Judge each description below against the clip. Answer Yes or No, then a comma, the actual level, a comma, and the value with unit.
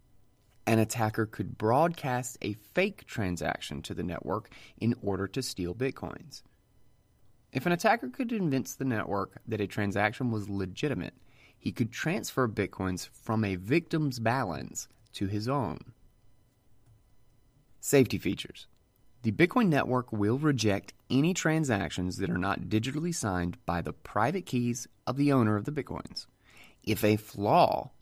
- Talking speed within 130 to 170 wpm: Yes, average, 140 wpm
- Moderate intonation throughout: Yes, average, 4.5 semitones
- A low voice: Yes, low, 115 Hz